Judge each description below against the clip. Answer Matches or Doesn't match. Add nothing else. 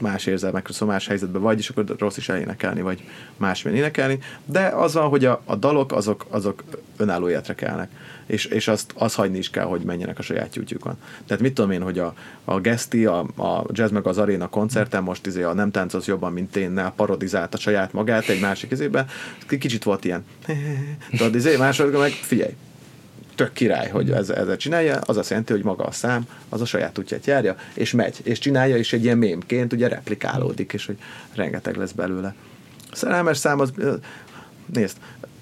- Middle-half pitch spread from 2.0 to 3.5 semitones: Doesn't match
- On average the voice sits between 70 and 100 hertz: Doesn't match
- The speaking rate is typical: Doesn't match